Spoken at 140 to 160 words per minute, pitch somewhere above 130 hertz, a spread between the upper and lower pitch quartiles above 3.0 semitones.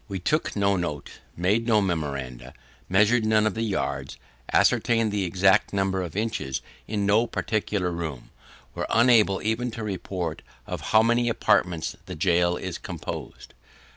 No: average, 150 wpm; low, 100 Hz; average, 3.9 semitones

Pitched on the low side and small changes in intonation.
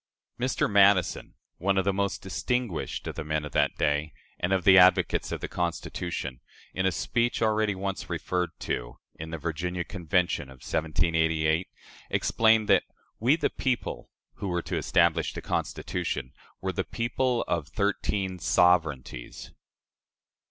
No: very low, 90 Hz; average, 3.9 semitones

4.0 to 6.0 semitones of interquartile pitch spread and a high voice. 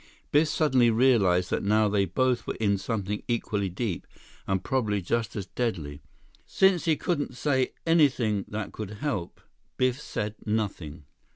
No: average, 4.7 semitones; low, 110 Hz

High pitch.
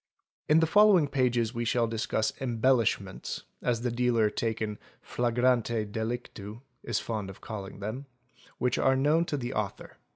No: low, 120 Hz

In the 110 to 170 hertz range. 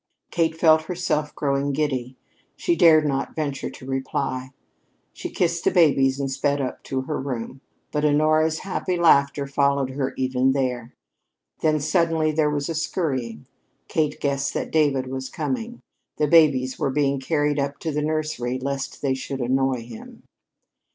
Yes: medium, 140 Hz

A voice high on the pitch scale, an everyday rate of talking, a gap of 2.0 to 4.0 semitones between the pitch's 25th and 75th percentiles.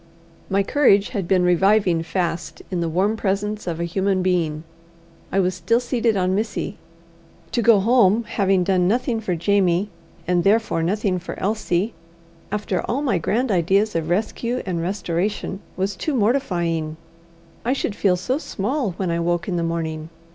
Yes: high, 195 Hz; average, 165 wpm; average, 3.7 semitones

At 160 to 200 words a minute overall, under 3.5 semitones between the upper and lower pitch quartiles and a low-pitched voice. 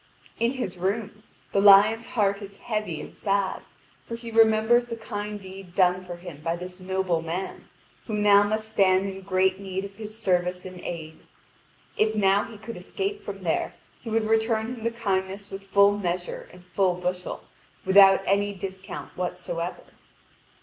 No: average, 170 wpm; average, 2.8 semitones; high, 195 Hz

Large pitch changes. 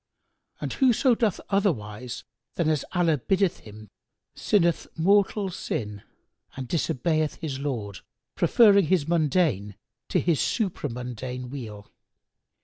Yes: wide, 7.3 semitones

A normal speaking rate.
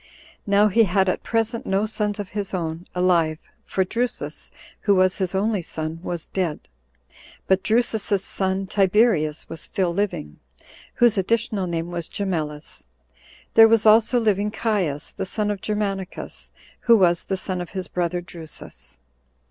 Yes: average, 155 wpm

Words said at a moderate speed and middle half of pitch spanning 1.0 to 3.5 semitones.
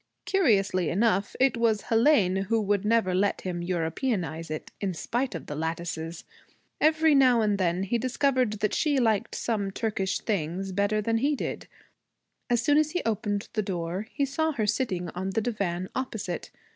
No: average, 170 wpm; average, 4.8 semitones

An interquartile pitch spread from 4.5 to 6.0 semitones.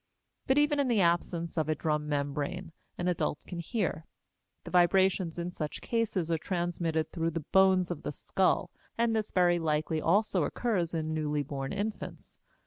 No: average, 3.4 semitones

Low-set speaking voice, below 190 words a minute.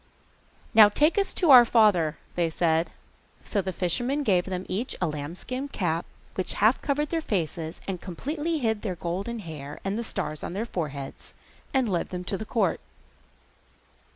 No: high, 195 Hz; average, 170 wpm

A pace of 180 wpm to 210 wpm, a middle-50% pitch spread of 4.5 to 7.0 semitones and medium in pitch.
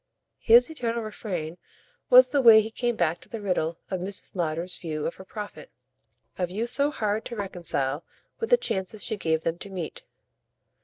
No: average, 185 wpm; average, 5.1 semitones; high, 200 Hz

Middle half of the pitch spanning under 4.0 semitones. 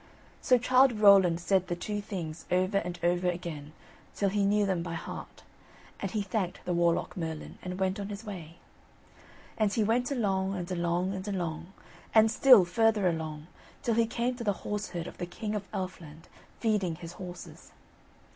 Yes: average, 3.2 semitones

